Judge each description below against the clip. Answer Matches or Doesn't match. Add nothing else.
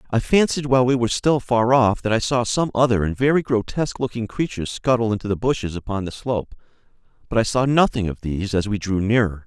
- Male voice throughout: Matches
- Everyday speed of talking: Doesn't match